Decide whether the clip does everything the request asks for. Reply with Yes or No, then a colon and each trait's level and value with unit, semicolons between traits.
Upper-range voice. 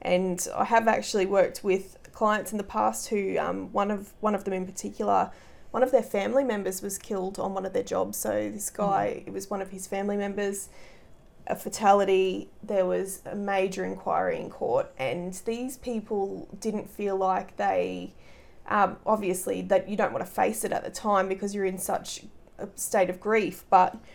Yes: high, 195 Hz